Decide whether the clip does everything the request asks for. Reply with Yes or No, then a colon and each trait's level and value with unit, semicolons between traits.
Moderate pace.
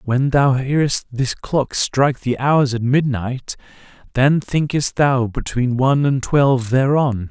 Yes: average, 150 wpm